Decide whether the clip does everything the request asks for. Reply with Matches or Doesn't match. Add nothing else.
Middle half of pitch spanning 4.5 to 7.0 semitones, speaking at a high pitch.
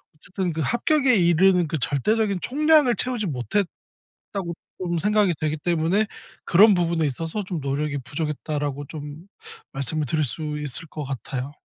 Doesn't match